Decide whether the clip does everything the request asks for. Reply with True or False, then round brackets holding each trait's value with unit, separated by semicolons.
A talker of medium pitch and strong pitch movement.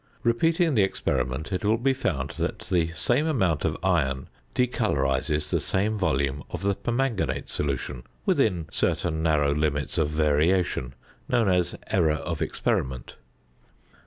False (85 Hz; 6.3 semitones)